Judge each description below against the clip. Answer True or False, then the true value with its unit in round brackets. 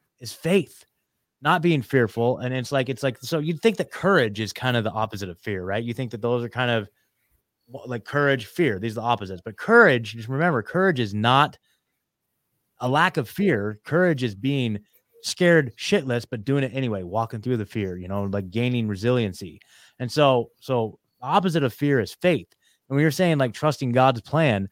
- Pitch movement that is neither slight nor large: True (4.4 semitones)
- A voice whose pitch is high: False (125 Hz)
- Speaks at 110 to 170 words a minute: False (200 wpm)